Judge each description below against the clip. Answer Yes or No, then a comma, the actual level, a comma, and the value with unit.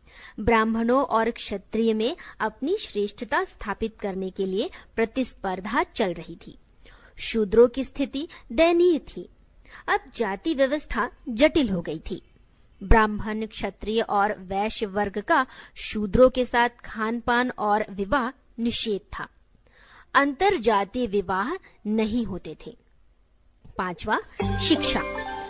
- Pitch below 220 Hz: No, high, 225 Hz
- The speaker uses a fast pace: No, average, 115 wpm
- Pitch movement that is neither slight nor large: Yes, average, 4.2 semitones